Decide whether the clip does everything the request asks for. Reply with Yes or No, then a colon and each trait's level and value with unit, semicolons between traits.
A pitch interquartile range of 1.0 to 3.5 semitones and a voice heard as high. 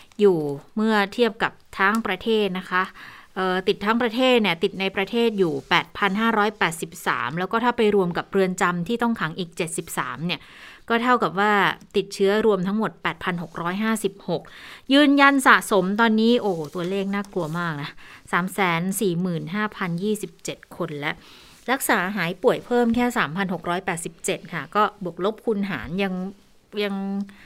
Yes: average, 3.1 semitones; high, 195 Hz